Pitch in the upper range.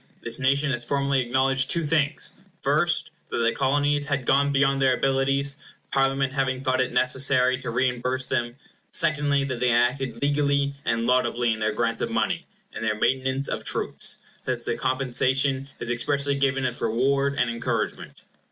No: low, 135 Hz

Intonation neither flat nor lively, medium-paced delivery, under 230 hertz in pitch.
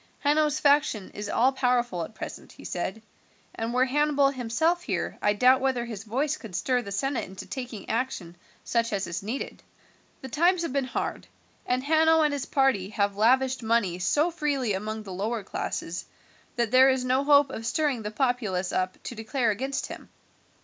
No: average, 4.6 semitones; average, 185 wpm; very high, 250 Hz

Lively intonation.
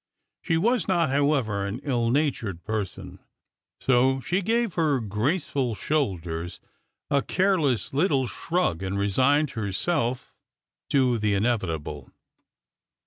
Yes: wide, 7.1 semitones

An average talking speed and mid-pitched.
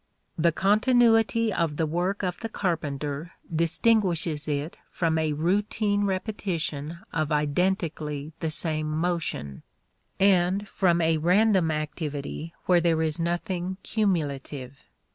No: slow, 115 wpm; medium, 170 Hz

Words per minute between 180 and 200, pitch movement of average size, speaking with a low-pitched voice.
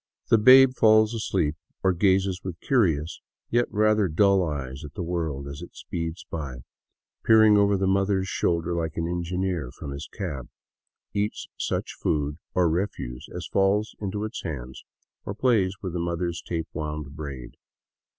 No: average, 160 wpm; average, 4.7 semitones; very low, 90 Hz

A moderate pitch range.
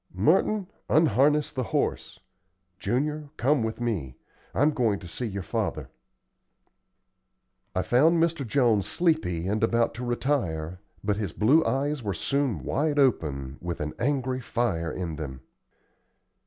No: wide, 7.7 semitones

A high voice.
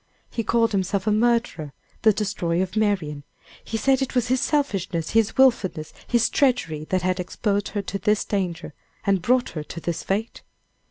Yes: high, 205 Hz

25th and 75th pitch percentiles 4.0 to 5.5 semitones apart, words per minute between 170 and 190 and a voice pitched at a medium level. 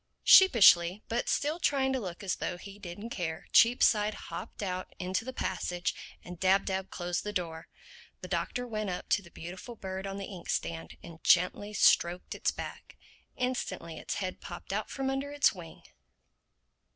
No: average, 4.3 semitones; average, 175 wpm; high, 195 Hz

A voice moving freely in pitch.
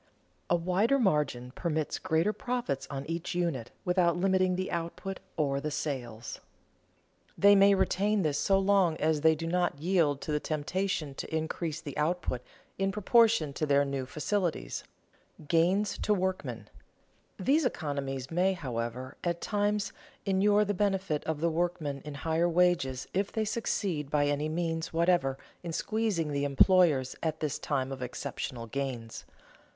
No: average, 4.8 semitones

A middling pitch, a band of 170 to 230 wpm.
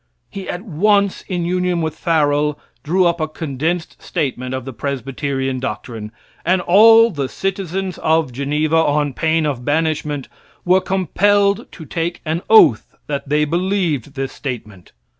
No: medium, 160 Hz; average, 145 wpm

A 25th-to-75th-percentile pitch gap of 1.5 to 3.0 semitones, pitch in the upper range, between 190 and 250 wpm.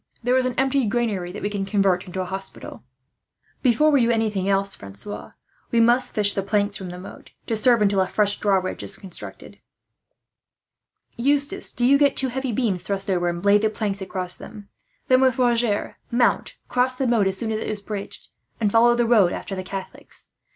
No: average, 3.8 semitones; high, 210 Hz; average, 200 wpm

